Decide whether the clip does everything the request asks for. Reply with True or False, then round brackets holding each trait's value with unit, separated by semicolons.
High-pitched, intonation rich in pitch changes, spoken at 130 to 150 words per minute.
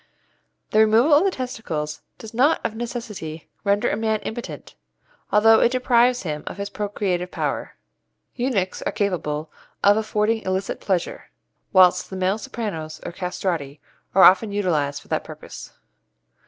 False (200 Hz; 3.8 semitones; 145 wpm)